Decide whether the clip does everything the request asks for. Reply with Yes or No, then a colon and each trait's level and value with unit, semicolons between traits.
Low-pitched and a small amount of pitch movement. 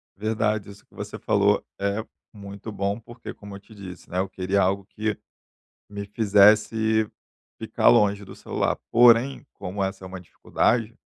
Yes: low, 100 Hz; narrow, 1.9 semitones